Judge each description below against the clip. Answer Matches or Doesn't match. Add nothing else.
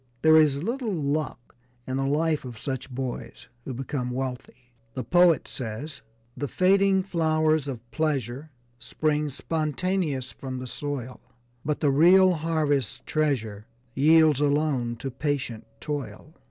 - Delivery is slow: Matches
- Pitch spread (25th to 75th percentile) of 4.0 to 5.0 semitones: Doesn't match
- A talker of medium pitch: Matches